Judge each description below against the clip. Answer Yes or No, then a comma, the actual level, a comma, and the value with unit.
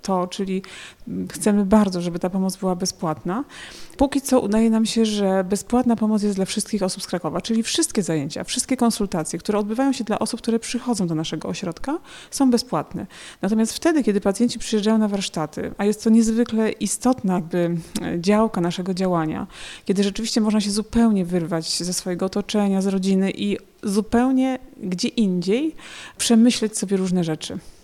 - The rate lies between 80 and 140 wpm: No, fast, 160 wpm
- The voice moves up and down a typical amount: Yes, average, 3.7 semitones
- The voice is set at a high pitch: Yes, high, 205 Hz